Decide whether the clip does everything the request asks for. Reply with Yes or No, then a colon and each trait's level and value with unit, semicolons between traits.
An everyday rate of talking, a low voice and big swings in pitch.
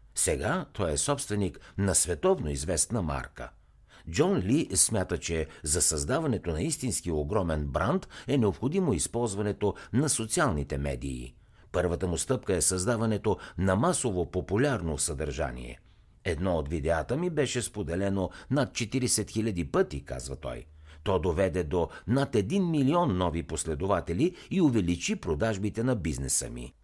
Yes: average, 130 wpm; very low, 95 Hz; wide, 7.4 semitones